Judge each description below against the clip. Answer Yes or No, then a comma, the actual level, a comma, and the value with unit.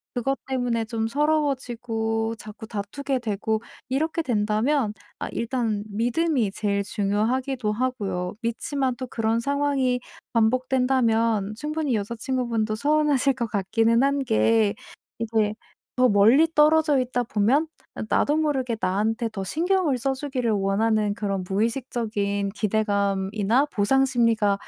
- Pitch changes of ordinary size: Yes, average, 3.9 semitones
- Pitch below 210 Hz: No, high, 230 Hz